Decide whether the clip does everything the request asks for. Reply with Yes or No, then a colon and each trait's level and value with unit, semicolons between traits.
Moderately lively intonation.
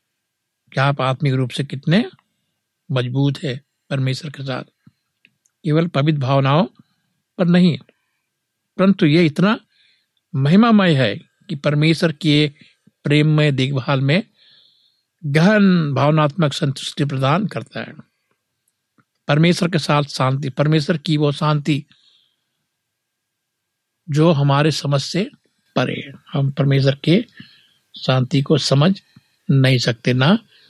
Yes: average, 3.9 semitones